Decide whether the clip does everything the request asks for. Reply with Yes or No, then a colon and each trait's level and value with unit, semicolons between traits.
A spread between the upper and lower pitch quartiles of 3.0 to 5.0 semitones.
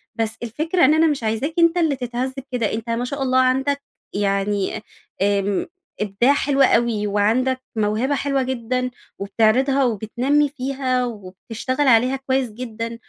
Yes: average, 3.6 semitones